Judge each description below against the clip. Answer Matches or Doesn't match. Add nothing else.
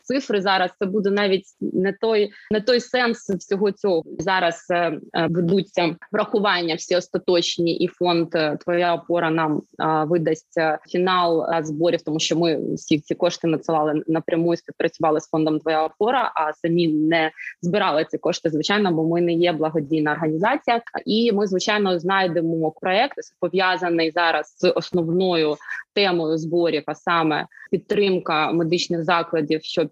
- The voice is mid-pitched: Matches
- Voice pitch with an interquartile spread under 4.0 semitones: Matches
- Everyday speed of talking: Matches